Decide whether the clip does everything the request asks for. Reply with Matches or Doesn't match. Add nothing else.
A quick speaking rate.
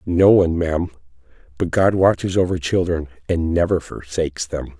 Doesn't match